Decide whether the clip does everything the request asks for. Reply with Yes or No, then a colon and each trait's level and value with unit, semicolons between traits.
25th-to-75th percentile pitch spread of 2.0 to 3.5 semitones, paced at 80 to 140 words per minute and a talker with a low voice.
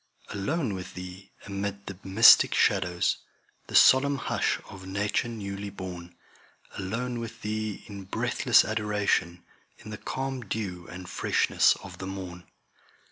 Yes: average, 2.7 semitones; slow, 135 wpm; low, 100 Hz